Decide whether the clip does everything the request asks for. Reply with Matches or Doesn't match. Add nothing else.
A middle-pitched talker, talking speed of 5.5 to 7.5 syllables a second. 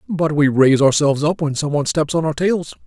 Matches